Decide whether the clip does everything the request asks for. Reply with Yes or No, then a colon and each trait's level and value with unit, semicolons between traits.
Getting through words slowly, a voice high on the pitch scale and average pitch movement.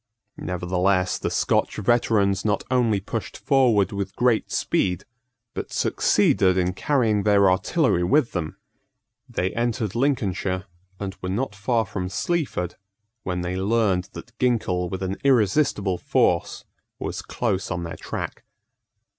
No: slow, 130 wpm; low, 100 Hz; average, 4.2 semitones